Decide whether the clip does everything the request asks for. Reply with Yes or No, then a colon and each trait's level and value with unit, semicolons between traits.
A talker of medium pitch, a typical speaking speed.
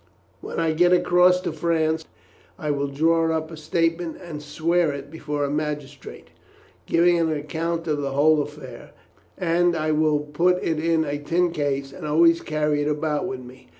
Yes: medium, 155 Hz; average, 180 wpm